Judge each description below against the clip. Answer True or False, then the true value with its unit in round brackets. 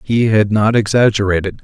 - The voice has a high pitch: False (105 Hz)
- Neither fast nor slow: True (145 wpm)